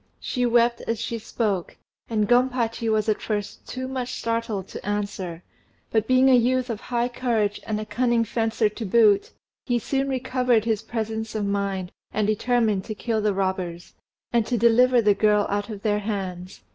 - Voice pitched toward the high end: Yes, high, 220 Hz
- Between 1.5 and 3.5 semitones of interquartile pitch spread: Yes, average, 2.7 semitones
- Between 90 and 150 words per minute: No, average, 180 wpm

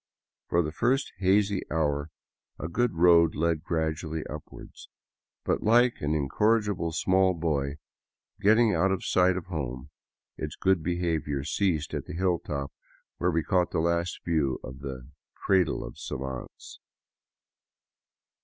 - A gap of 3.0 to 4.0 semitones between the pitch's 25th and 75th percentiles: Yes, average, 3.7 semitones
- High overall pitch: No, very low, 85 Hz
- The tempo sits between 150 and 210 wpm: No, slow, 135 wpm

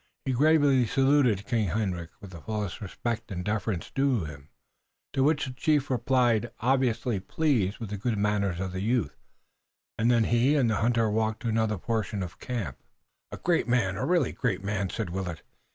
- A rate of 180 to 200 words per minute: Yes, average, 185 wpm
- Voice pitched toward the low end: Yes, low, 110 Hz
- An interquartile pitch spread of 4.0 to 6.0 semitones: Yes, average, 4.6 semitones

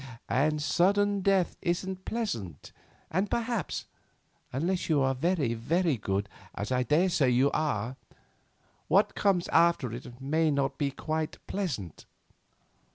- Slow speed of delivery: Yes, slow, 115 wpm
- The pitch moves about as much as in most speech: No, wide, 6.4 semitones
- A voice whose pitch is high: No, medium, 155 Hz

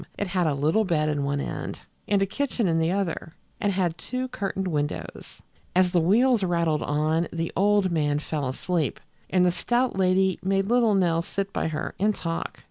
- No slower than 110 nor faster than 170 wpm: No, average, 195 wpm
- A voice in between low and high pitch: Yes, medium, 180 Hz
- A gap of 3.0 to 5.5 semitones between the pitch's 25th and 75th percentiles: Yes, average, 3.6 semitones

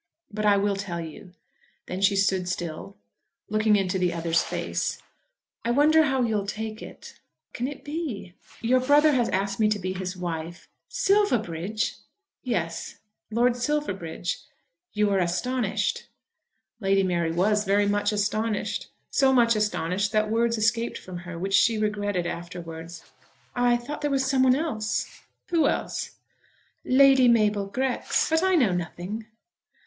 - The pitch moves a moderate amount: Yes, average, 5.0 semitones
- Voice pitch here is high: Yes, high, 210 Hz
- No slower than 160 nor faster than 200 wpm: No, average, 150 wpm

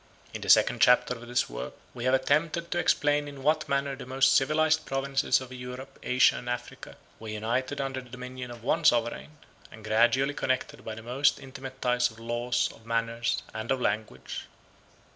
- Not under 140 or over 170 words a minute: No, average, 185 wpm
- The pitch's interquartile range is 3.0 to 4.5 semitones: No, narrow, 2.5 semitones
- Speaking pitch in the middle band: No, low, 125 Hz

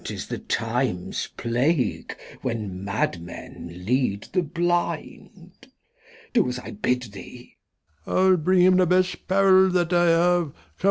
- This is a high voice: No, medium, 170 Hz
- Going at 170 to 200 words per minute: No, average, 145 wpm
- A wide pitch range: Yes, wide, 6.6 semitones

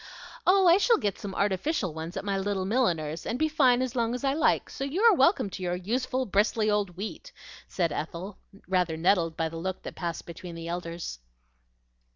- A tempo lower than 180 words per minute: No, average, 200 wpm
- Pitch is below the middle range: No, high, 195 Hz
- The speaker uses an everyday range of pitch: No, wide, 6.8 semitones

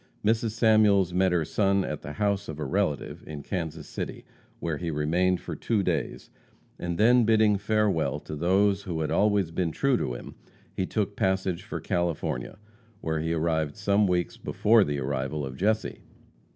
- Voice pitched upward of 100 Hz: No, very low, 90 Hz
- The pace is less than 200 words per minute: Yes, average, 175 wpm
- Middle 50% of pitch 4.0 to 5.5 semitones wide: Yes, average, 4.5 semitones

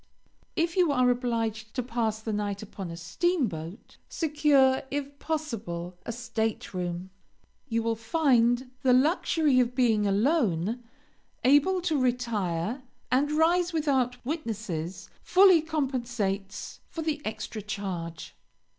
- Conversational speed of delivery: No, slow, 120 wpm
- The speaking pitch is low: No, high, 245 Hz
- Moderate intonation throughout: No, wide, 5.9 semitones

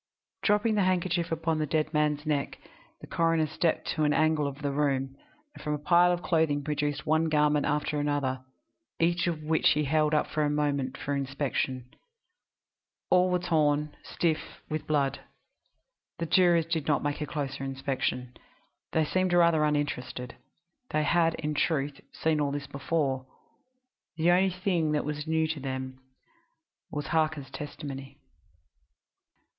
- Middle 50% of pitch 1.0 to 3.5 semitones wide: Yes, narrow, 2.4 semitones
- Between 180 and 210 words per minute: No, average, 155 wpm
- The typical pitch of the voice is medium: Yes, medium, 150 Hz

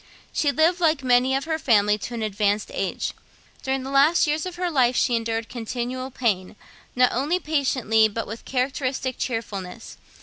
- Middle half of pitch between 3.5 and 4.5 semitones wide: Yes, average, 3.9 semitones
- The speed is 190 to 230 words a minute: No, average, 170 wpm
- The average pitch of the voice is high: Yes, very high, 255 Hz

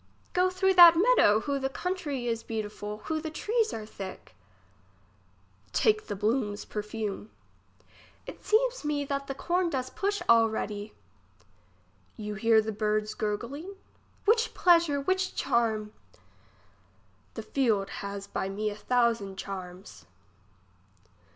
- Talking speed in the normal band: No, slow, 125 wpm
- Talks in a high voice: Yes, high, 230 Hz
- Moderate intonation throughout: No, wide, 7.9 semitones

